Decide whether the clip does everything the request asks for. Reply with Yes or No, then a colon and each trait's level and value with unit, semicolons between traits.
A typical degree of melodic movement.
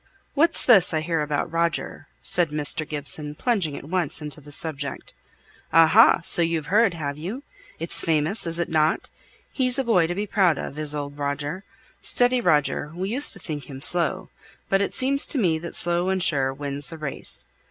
Yes: average, 4.3 semitones